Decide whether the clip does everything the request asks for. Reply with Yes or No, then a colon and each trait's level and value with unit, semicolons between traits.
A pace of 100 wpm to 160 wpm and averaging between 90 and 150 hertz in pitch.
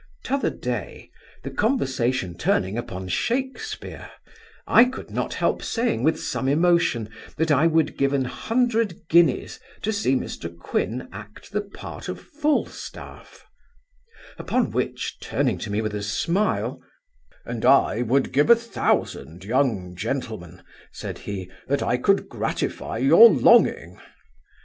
Yes: slow, 135 wpm; medium, 140 Hz